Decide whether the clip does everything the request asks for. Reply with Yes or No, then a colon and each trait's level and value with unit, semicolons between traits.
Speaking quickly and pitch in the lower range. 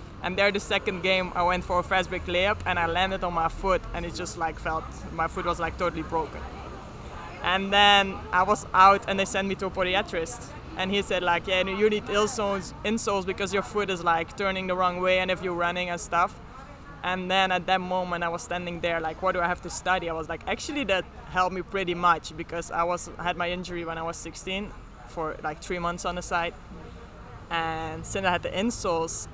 No: fast, 230 wpm; medium, 180 Hz